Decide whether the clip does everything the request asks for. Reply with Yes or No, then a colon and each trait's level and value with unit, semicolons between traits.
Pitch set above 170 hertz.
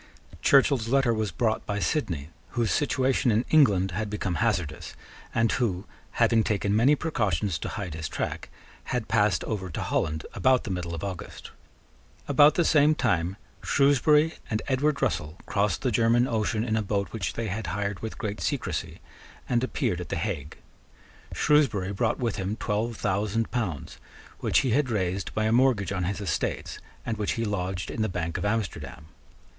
No: low, 105 Hz